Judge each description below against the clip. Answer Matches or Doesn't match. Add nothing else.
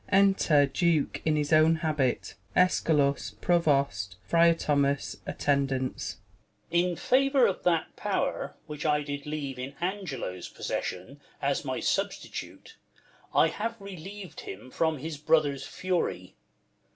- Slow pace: Matches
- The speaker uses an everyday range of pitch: Matches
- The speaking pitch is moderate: Matches